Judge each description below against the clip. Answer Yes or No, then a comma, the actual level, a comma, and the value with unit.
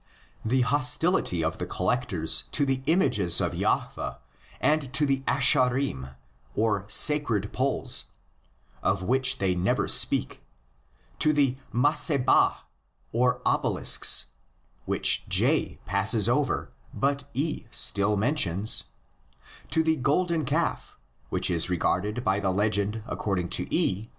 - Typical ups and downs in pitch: No, wide, 6.3 semitones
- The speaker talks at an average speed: No, slow, 120 wpm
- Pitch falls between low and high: No, low, 125 Hz